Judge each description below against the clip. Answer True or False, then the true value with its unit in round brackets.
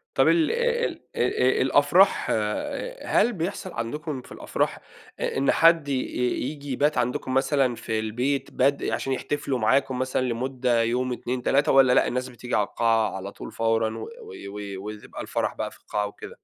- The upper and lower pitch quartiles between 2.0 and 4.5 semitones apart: True (3.6 semitones)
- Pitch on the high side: False (130 Hz)